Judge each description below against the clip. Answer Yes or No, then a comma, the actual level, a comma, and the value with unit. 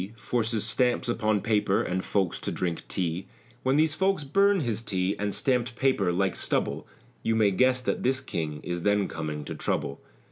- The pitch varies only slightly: No, wide, 5.6 semitones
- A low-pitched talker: Yes, low, 110 Hz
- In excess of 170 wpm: Yes, average, 180 wpm